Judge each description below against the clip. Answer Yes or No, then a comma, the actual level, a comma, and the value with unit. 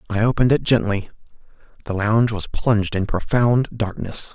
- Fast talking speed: No, average, 150 wpm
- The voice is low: Yes, low, 110 Hz